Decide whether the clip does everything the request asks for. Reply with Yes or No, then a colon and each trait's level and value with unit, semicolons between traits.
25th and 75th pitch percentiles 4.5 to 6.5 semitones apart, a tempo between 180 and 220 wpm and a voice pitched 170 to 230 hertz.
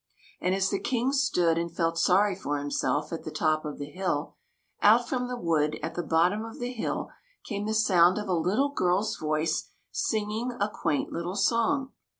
Yes: average, 5.1 semitones; average, 195 wpm; medium, 185 Hz